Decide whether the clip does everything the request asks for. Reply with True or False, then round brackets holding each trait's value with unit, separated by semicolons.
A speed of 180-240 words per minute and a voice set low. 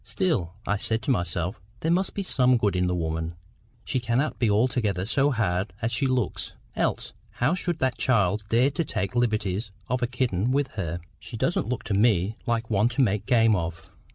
True (200 wpm; 115 Hz)